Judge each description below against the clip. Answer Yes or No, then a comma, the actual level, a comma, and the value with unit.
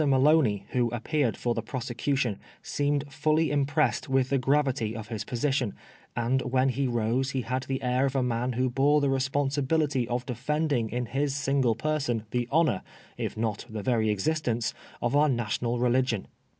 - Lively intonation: No, average, 3.1 semitones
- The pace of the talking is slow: No, average, 170 wpm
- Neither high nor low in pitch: No, low, 130 Hz